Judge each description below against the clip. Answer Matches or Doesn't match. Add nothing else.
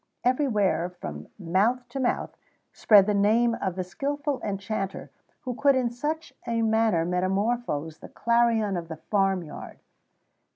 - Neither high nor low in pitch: Doesn't match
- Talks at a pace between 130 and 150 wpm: Matches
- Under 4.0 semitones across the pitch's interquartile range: Doesn't match